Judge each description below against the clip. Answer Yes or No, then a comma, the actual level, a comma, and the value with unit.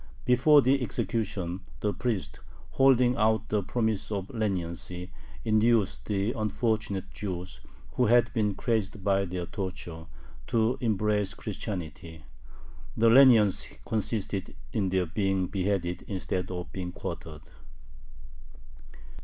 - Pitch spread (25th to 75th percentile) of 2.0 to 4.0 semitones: Yes, average, 3.4 semitones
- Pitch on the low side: Yes, low, 100 Hz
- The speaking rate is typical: No, slow, 110 wpm